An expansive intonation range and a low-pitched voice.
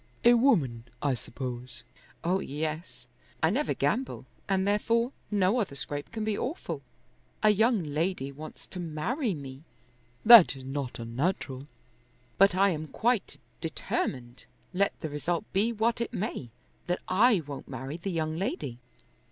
No: wide, 7.2 semitones; medium, 170 Hz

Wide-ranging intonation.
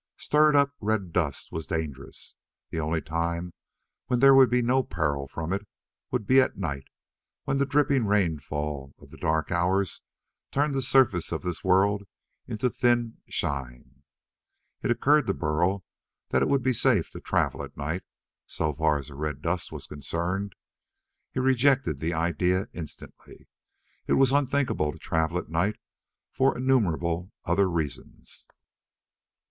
Yes: wide, 7.9 semitones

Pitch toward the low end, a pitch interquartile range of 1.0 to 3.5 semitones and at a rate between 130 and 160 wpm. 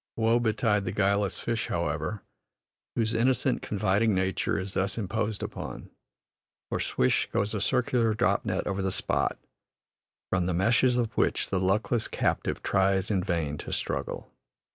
Yes: low, 100 Hz; average, 3.1 semitones; average, 150 wpm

